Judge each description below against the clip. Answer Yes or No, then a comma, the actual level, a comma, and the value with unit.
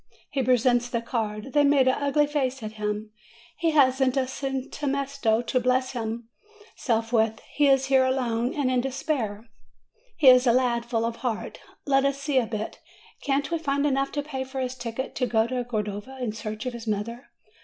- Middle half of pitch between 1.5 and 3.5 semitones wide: Yes, average, 3.0 semitones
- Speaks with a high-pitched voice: Yes, very high, 255 Hz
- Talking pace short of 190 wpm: No, average, 195 wpm